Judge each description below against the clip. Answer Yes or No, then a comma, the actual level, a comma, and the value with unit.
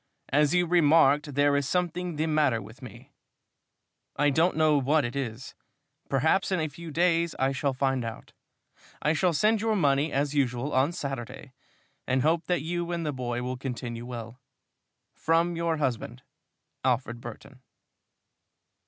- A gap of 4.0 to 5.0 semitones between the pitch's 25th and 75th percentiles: Yes, average, 4.3 semitones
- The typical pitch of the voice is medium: Yes, medium, 145 Hz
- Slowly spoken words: No, average, 155 wpm